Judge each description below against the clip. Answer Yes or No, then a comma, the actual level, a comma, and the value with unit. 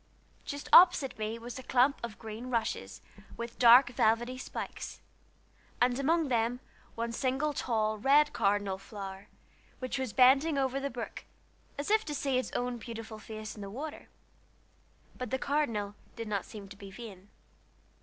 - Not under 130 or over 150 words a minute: No, average, 160 wpm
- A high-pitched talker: Yes, high, 240 Hz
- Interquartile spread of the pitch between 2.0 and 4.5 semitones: Yes, average, 3.7 semitones